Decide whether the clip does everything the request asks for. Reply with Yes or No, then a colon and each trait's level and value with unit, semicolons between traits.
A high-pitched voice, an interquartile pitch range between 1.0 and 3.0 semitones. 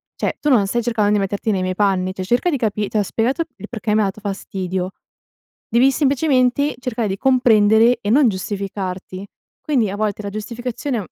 No: high, 215 Hz; average, 3.9 semitones